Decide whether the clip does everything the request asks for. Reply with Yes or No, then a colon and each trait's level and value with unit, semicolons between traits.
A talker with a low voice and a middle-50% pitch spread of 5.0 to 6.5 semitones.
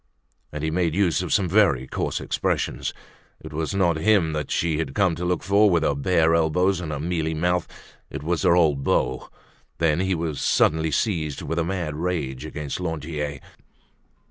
No: very low, 80 Hz; average, 2.8 semitones